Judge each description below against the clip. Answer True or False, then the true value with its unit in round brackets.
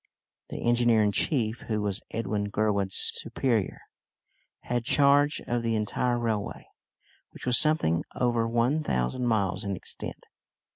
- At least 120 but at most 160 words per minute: True (135 wpm)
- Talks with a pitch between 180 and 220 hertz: False (115 Hz)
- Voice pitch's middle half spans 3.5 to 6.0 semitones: False (2.9 semitones)